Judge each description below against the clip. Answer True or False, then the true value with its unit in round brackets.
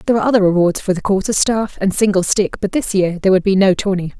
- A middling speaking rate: False (270 wpm)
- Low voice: False (195 Hz)